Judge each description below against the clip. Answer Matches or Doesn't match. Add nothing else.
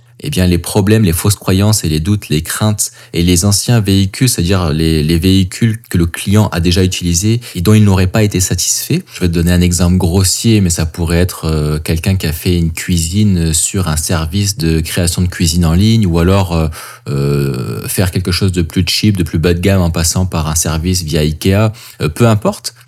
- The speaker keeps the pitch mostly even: Doesn't match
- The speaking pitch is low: Matches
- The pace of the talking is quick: Matches